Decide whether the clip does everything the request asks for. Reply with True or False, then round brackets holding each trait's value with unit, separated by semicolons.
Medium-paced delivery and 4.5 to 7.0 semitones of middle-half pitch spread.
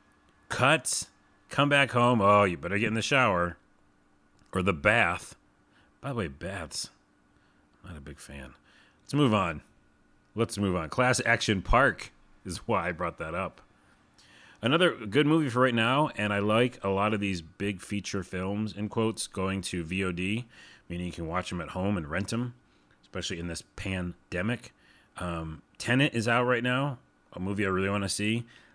True (175 wpm; 5.0 semitones)